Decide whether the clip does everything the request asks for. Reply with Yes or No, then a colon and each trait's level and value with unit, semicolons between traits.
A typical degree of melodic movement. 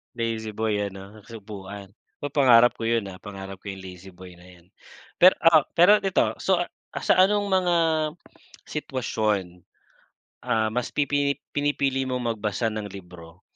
No: wide, 6.5 semitones